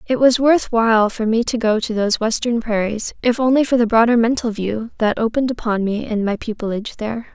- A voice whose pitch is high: Yes, high, 225 Hz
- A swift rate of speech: Yes, fast, 220 wpm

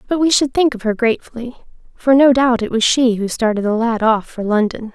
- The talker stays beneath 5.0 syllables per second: No, 5.6 syllables/s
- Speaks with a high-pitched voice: Yes, high, 235 Hz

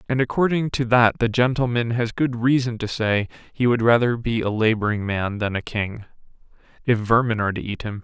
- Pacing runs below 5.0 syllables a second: No, 5.4 syllables/s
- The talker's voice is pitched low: Yes, low, 115 Hz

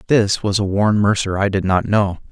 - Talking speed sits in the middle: No, fast, 235 wpm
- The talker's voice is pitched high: No, low, 100 Hz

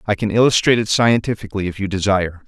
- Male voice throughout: Yes, male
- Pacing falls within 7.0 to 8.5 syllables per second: Yes, 7.3 syllables/s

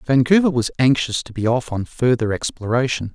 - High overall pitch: No, low, 125 Hz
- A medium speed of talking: Yes, average, 170 wpm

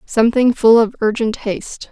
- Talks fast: No, average, 155 wpm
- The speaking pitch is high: Yes, high, 230 Hz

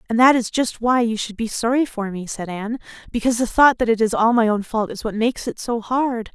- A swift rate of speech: Yes, fast, 275 wpm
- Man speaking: No, female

